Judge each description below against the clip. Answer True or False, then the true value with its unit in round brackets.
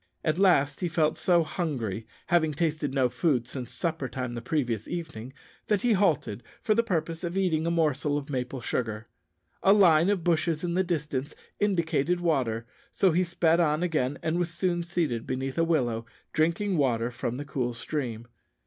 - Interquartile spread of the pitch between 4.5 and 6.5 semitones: True (5.1 semitones)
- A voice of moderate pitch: True (155 Hz)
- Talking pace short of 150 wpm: False (180 wpm)